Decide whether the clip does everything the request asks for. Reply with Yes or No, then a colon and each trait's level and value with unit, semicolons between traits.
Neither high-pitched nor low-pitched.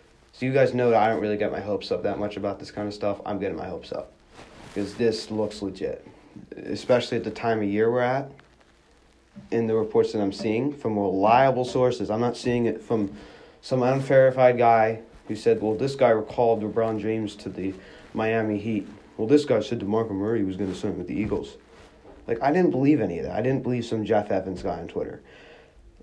No: low, 110 Hz